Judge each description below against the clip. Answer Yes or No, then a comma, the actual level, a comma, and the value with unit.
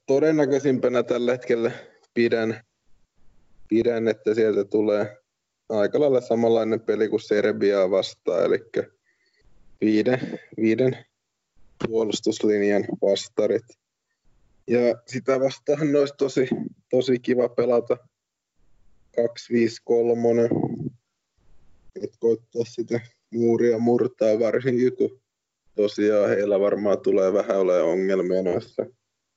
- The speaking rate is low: Yes, slow, 90 wpm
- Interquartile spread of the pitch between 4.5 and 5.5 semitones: No, average, 3.0 semitones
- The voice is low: Yes, low, 115 Hz